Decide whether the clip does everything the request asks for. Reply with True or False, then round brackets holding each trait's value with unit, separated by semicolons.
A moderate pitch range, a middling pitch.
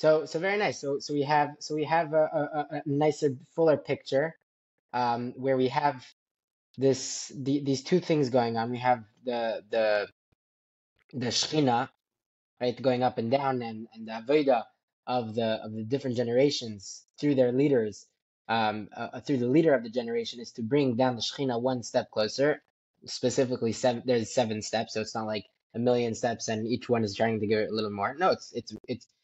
False (3.9 semitones; 125 Hz)